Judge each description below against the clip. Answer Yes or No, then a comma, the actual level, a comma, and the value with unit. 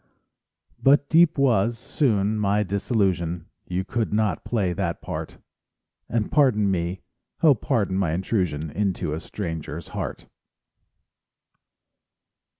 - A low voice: Yes, low, 100 Hz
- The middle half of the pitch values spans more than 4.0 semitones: Yes, average, 4.5 semitones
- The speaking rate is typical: No, slow, 110 wpm